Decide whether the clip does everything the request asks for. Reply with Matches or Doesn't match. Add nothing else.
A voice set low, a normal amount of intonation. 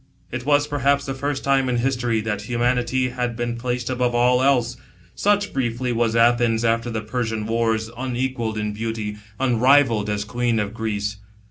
Doesn't match